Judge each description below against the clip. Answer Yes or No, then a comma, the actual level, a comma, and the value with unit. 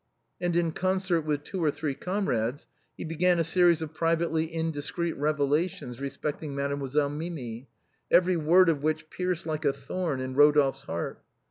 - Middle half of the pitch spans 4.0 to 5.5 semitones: No, average, 3.2 semitones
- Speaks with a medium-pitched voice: Yes, medium, 155 Hz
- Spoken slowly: No, average, 160 wpm